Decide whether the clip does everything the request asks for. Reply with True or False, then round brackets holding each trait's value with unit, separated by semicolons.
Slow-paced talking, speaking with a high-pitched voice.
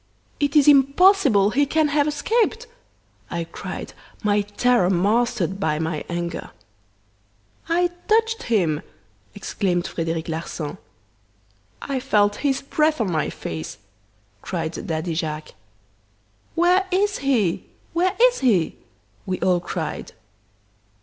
True (115 wpm; 220 Hz)